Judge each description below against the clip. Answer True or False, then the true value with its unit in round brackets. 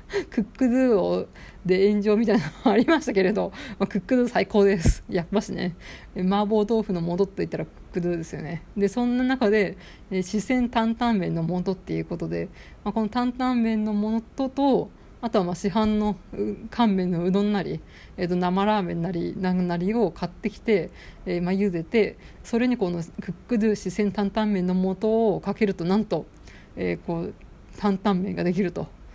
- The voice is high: True (205 Hz)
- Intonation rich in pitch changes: False (3.4 semitones)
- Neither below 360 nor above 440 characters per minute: True (365 characters per minute)